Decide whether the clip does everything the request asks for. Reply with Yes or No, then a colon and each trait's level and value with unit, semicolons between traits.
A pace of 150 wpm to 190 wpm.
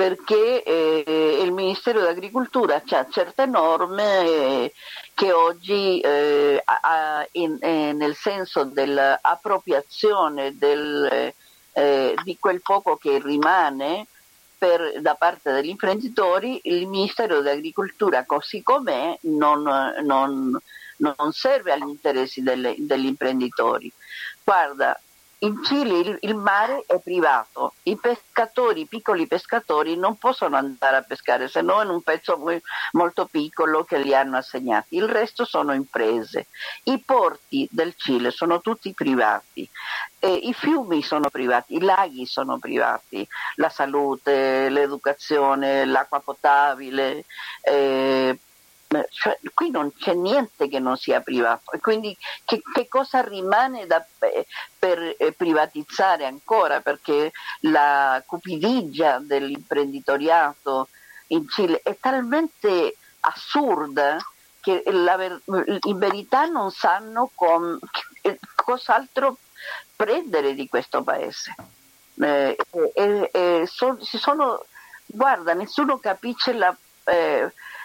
No: slow, 115 wpm